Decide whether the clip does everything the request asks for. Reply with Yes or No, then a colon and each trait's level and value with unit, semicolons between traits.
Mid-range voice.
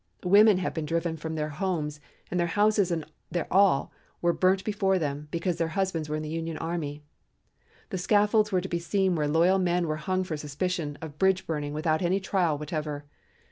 Yes: medium, 170 Hz